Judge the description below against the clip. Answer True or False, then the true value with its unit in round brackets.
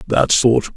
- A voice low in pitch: True (120 Hz)